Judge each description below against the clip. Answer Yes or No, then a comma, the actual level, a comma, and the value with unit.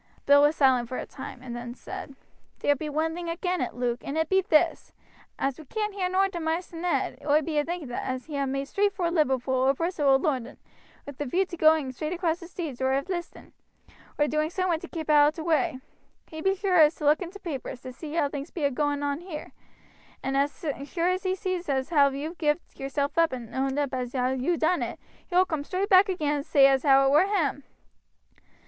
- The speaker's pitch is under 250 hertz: No, very high, 305 Hz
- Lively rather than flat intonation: No, average, 4.2 semitones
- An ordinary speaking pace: No, fast, 240 wpm